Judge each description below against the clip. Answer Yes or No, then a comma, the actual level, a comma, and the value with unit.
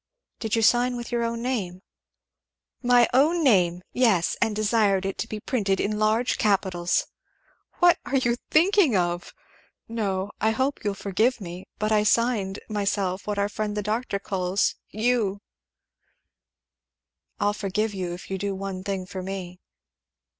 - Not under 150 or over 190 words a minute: Yes, average, 155 wpm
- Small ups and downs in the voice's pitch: No, average, 3.4 semitones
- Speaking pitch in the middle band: No, high, 210 Hz